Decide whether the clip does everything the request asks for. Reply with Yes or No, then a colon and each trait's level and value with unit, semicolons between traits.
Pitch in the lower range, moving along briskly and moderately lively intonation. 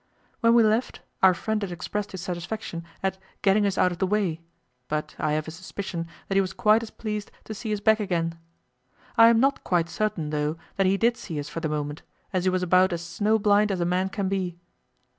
No: high, 190 Hz; fast, 230 wpm; average, 3.8 semitones